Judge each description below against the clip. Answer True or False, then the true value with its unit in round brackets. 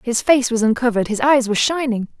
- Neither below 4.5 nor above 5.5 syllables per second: False (6.4 syllables/s)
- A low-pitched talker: False (245 Hz)